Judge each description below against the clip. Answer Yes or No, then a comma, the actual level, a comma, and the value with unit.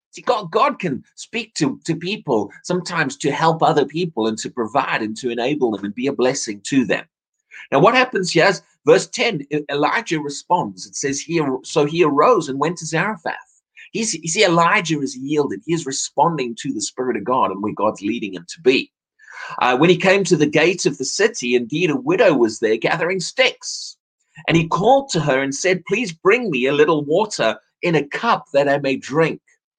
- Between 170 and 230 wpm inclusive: Yes, fast, 205 wpm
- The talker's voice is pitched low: No, medium, 155 Hz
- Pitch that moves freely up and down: Yes, wide, 5.8 semitones